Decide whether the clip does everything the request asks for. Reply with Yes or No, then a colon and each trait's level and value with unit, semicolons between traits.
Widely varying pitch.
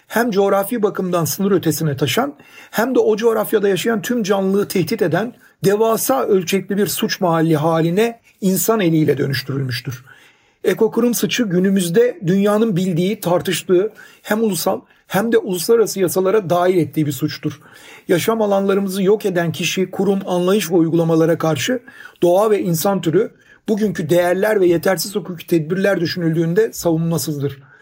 No: average, 4.0 semitones